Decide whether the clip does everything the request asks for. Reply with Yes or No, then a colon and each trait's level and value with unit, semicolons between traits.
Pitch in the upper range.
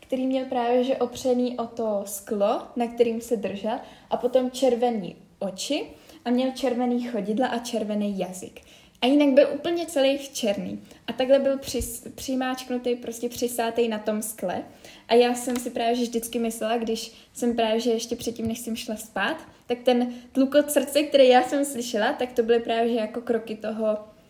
Yes: high, 240 Hz